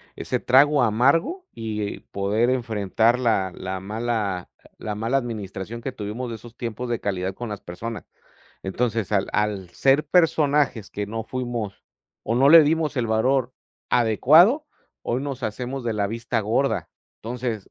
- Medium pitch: No, low, 115 Hz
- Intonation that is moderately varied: Yes, average, 3.7 semitones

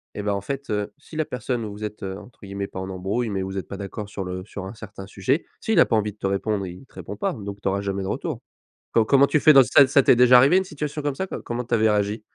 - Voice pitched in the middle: No, low, 105 Hz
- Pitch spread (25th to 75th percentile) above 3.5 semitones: Yes, average, 5.1 semitones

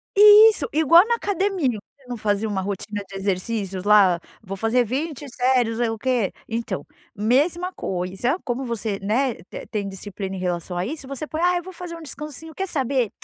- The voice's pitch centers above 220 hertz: Yes, high, 240 Hz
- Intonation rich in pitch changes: Yes, wide, 7.5 semitones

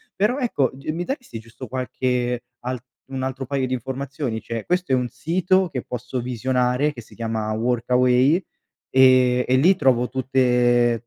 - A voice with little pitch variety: Yes, narrow, 1.9 semitones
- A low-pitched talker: Yes, low, 130 Hz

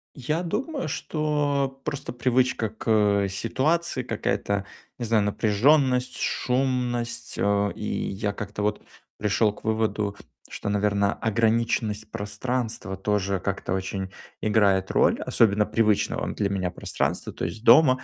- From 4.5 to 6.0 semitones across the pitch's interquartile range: No, average, 3.9 semitones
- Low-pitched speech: Yes, low, 110 Hz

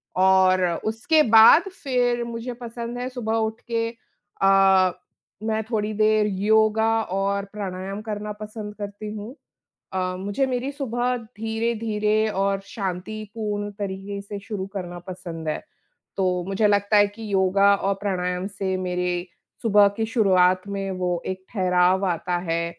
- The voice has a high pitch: Yes, high, 205 Hz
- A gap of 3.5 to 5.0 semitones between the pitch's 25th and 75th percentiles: No, average, 2.8 semitones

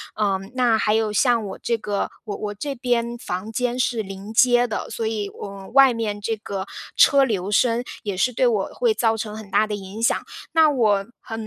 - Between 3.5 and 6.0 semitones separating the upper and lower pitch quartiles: No, average, 2.9 semitones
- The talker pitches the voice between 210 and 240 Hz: Yes, high, 220 Hz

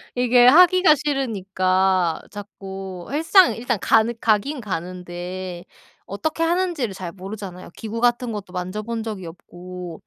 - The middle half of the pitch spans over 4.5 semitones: Yes, average, 5.2 semitones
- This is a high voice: Yes, high, 205 Hz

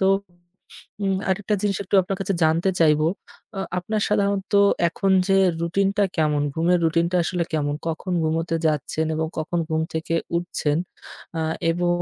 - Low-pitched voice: No, medium, 170 Hz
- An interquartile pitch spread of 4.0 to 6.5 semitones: No, average, 3.3 semitones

